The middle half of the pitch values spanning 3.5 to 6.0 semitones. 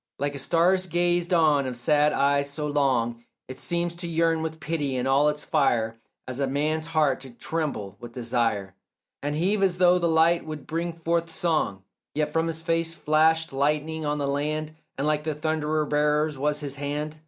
No: average, 2.7 semitones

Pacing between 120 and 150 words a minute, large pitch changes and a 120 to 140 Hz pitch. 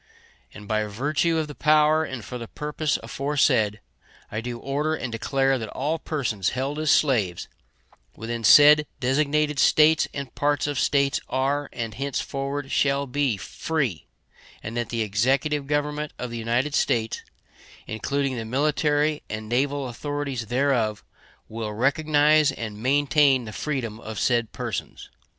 No: average, 145 wpm; average, 4.1 semitones; low, 135 Hz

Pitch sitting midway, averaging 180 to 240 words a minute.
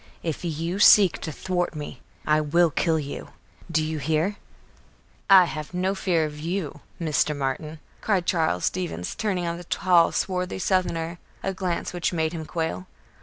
No: medium, 170 Hz; average, 165 wpm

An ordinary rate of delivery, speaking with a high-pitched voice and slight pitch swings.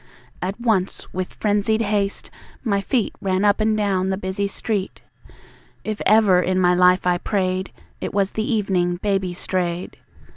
Yes: average, 155 wpm; high, 195 Hz; narrow, 2.2 semitones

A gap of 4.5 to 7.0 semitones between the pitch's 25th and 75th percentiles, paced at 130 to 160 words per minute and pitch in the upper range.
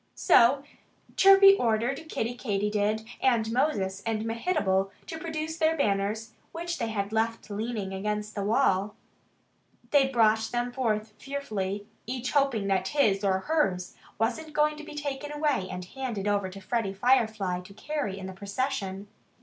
Yes: wide, 5.6 semitones; average, 150 wpm; high, 225 Hz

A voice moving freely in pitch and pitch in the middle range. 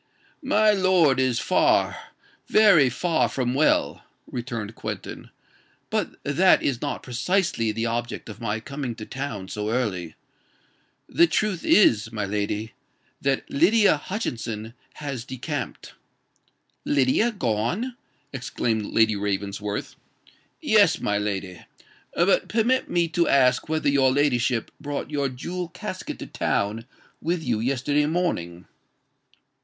No: wide, 6.9 semitones; low, 130 Hz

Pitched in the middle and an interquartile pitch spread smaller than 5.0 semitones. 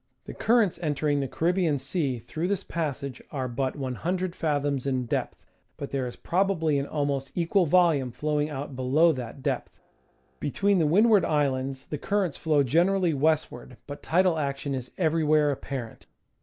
Yes: medium, 150 Hz; average, 3.8 semitones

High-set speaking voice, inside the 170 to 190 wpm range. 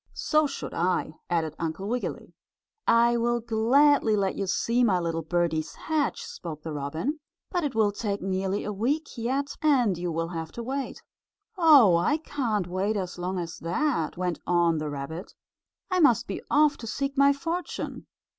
Yes: high, 210 Hz; average, 175 wpm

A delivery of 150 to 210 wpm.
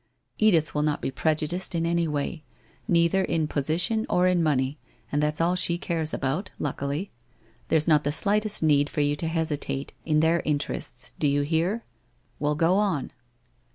Yes: average, 175 wpm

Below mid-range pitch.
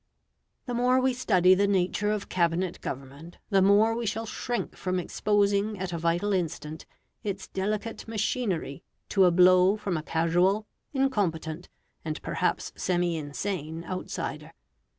No: medium, 185 Hz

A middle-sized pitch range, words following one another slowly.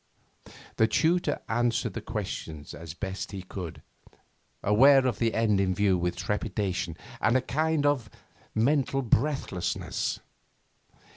No: wide, 6.2 semitones; slow, 125 wpm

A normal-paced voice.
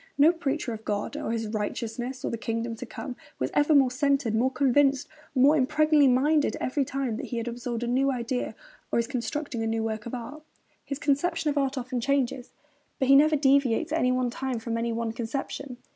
No: fast, 210 wpm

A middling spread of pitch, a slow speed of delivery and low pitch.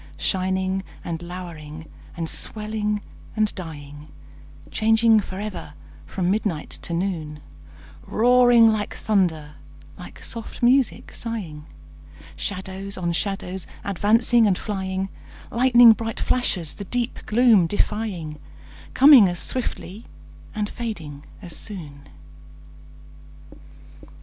No: average, 4.6 semitones; slow, 100 wpm; high, 195 Hz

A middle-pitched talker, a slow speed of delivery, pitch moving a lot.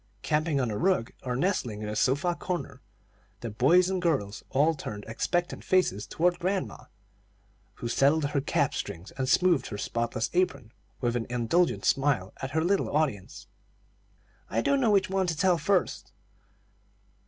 No: medium, 145 Hz; average, 160 wpm; wide, 7.2 semitones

